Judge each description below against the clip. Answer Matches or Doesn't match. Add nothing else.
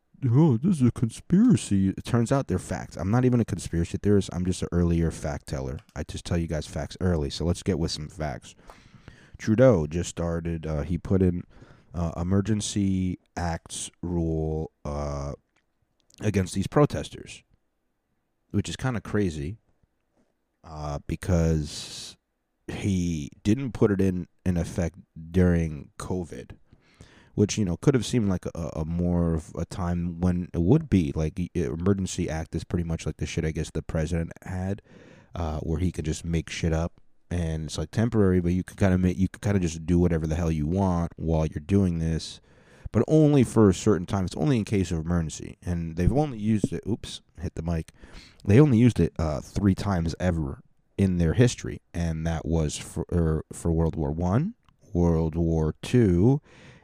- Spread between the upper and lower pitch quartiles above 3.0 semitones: Matches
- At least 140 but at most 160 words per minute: Doesn't match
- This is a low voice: Matches